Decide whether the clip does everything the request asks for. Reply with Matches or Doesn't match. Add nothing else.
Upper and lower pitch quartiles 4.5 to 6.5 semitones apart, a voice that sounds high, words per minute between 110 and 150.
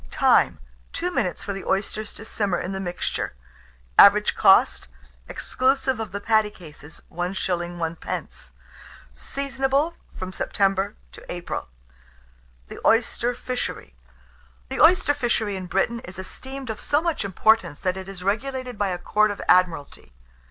Matches